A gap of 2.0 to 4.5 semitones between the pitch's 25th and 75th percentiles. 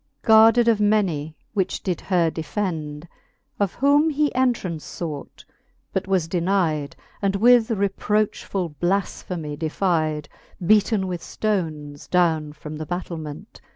No: average, 5.0 semitones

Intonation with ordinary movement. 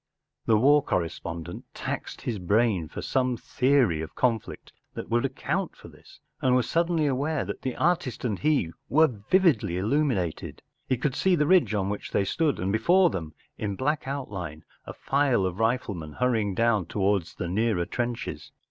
No: wide, 6.6 semitones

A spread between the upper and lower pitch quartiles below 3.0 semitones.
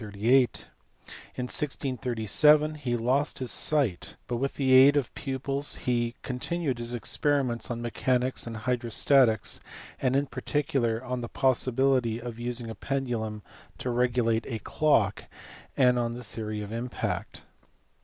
Yes: narrow, 2.6 semitones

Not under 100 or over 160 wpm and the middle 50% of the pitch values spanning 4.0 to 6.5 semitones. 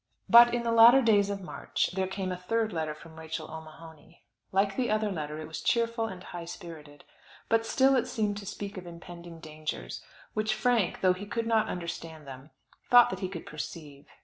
No: average, 200 wpm; wide, 5.4 semitones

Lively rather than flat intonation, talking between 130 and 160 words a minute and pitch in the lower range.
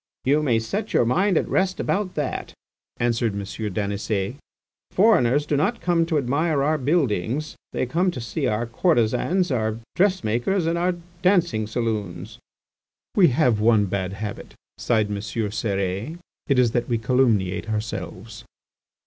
Yes: wide, 7.3 semitones; average, 145 wpm; low, 120 Hz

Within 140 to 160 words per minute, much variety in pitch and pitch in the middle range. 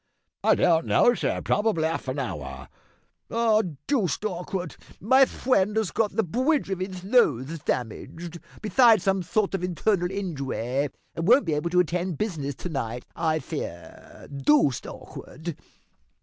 Yes: average, 150 wpm; wide, 6.2 semitones; medium, 180 Hz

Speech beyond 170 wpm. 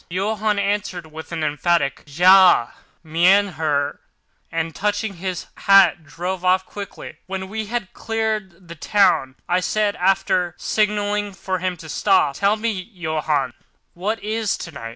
No: average, 140 wpm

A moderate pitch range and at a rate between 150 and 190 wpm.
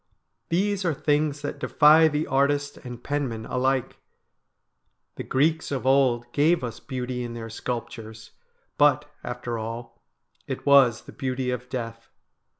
No: average, 3.4 semitones; average, 140 wpm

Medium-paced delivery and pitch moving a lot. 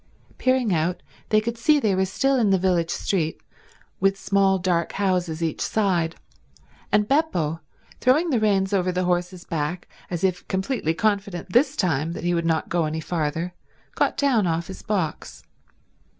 No: average, 165 wpm; average, 4.0 semitones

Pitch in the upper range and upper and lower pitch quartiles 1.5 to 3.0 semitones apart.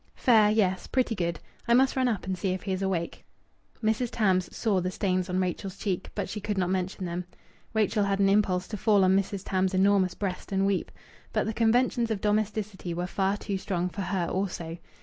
Yes: high, 195 Hz; narrow, 2.4 semitones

